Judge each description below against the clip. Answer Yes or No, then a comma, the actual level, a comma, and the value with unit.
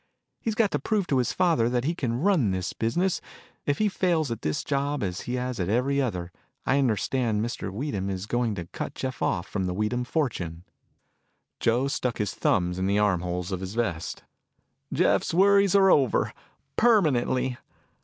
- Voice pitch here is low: Yes, low, 120 Hz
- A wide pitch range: Yes, wide, 6.8 semitones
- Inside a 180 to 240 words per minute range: Yes, average, 185 wpm